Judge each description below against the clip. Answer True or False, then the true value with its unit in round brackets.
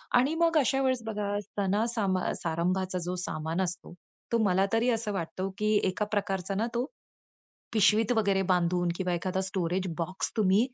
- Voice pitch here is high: True (195 Hz)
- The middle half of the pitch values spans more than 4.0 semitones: False (3.4 semitones)